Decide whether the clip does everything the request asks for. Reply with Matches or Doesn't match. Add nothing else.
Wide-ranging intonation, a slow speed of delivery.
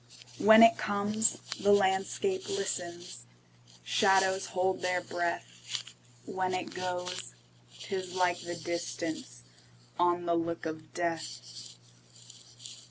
Matches